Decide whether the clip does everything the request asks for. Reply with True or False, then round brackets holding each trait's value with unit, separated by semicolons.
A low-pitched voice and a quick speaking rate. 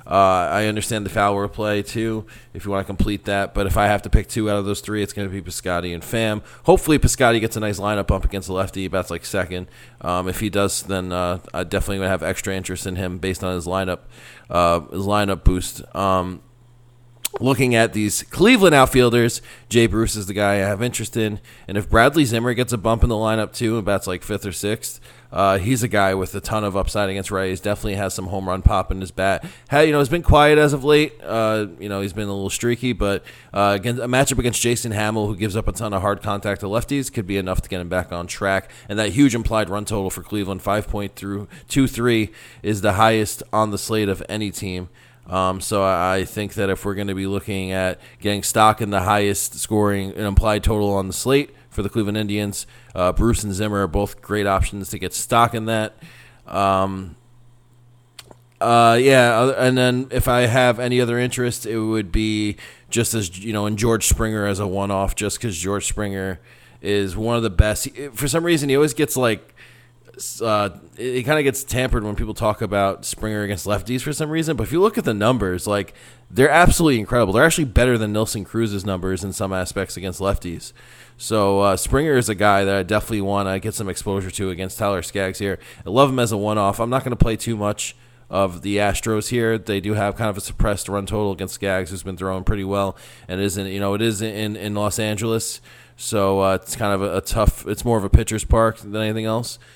True (105 Hz; 230 wpm)